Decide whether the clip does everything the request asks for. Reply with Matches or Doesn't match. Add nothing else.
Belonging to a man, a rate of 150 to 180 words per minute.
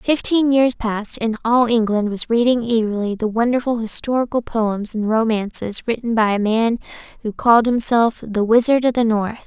Doesn't match